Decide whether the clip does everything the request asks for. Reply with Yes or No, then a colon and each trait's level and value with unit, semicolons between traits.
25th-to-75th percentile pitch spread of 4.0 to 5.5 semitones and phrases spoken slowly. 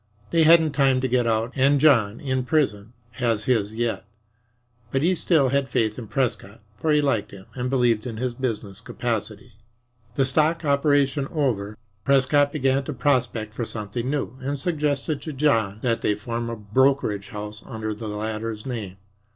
No: average, 4.3 semitones; average, 170 wpm